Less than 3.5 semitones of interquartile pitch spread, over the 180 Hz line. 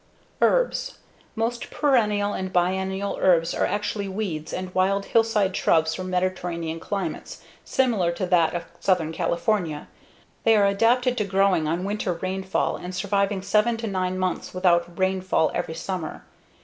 Yes: average, 2.7 semitones; high, 190 Hz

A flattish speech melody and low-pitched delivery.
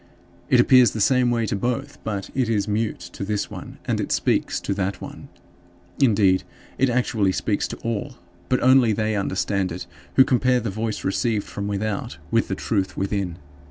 No: average, 3.6 semitones; low, 110 Hz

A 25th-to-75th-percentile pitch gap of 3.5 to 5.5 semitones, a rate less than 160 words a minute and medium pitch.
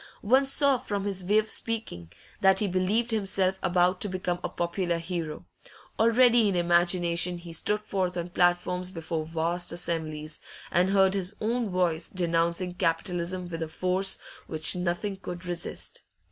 No: narrow, 2.4 semitones; average, 150 wpm; medium, 180 Hz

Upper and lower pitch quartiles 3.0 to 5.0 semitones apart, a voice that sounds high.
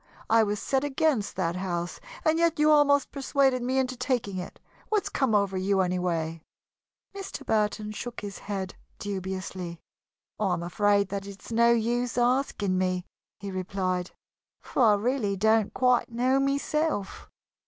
No: wide, 5.4 semitones; high, 210 Hz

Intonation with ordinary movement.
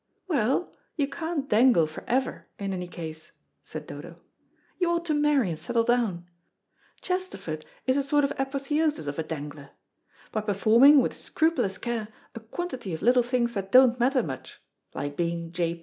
No: wide, 8.1 semitones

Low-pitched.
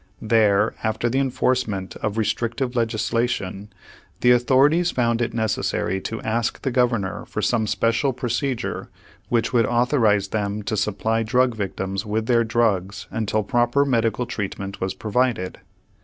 Yes: low, 115 Hz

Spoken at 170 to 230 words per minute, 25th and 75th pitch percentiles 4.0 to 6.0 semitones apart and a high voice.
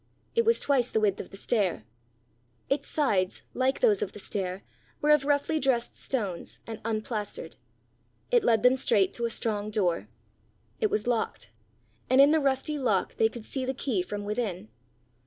Yes: average, 175 wpm; average, 4.8 semitones; high, 230 Hz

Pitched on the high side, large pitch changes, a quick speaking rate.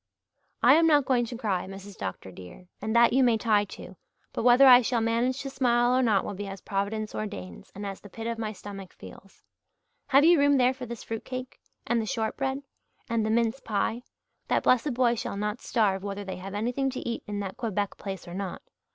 No: high, 225 Hz; average, 3.8 semitones; fast, 220 wpm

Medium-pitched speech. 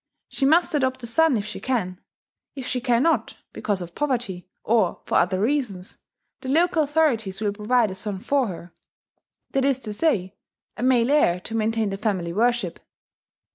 No: high, 230 Hz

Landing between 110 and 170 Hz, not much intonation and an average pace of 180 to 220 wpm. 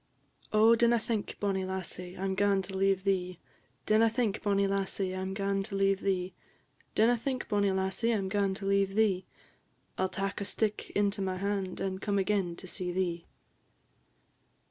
No: high, 195 Hz; narrow, 1.4 semitones; average, 190 wpm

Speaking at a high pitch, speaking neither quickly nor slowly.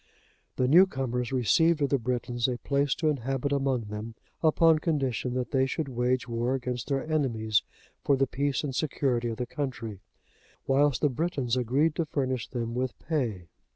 No: low, 130 Hz; average, 170 wpm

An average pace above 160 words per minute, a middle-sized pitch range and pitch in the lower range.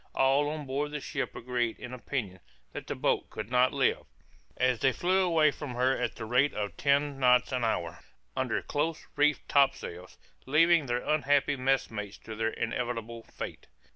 Yes: average, 170 wpm; average, 3.6 semitones; low, 130 Hz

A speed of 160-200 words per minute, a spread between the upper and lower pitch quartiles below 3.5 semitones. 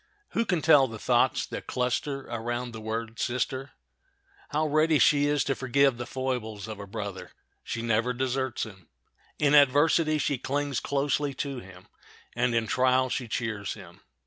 No: average, 165 wpm; average, 3.8 semitones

